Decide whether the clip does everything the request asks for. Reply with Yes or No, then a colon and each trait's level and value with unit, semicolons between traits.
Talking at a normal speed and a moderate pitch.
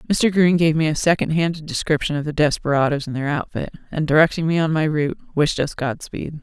No: fast, 215 wpm; medium, 155 Hz